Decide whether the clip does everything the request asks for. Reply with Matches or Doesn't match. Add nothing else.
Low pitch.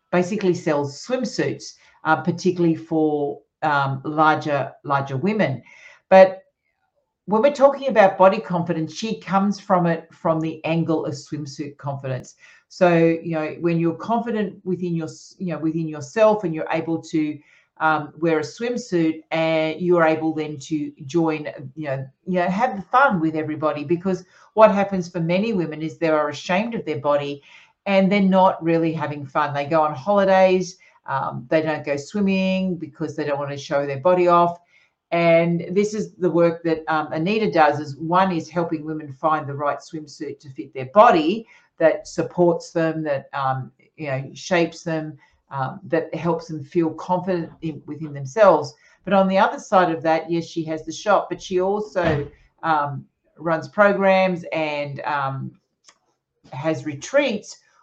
Doesn't match